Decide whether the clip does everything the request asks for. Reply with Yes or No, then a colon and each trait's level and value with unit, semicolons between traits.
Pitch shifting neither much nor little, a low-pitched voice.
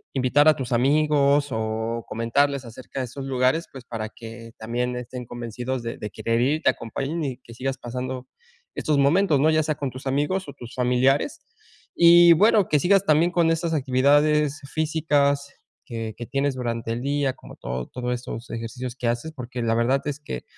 Yes: average, 3.7 semitones; low, 130 Hz